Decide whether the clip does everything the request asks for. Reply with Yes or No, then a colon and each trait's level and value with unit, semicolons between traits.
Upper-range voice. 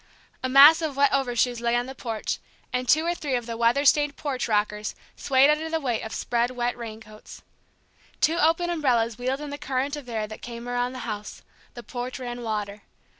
Yes: very high, 250 Hz